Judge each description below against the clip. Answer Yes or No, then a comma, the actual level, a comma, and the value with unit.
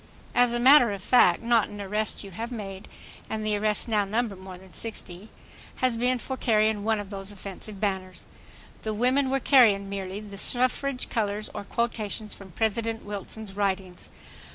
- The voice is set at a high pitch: Yes, high, 215 Hz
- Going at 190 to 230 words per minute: No, average, 165 wpm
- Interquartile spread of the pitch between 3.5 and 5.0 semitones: No, average, 3.0 semitones